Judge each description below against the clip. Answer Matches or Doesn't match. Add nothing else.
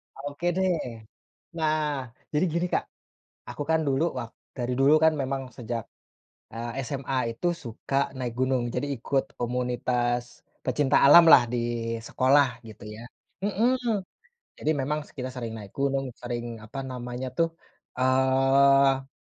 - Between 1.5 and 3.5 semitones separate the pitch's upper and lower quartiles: Matches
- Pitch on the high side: Doesn't match